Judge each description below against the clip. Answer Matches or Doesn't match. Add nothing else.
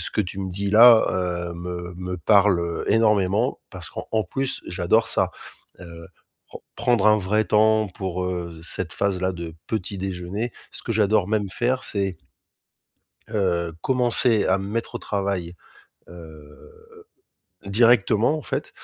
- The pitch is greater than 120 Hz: Doesn't match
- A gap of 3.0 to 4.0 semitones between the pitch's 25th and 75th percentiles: Matches